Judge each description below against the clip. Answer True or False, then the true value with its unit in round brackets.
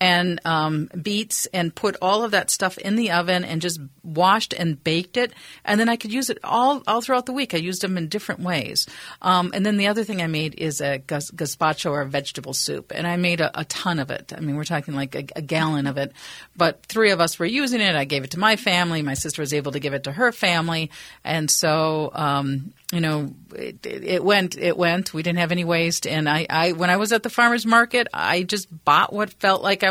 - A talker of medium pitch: True (175 Hz)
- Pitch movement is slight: False (4.8 semitones)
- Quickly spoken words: True (250 wpm)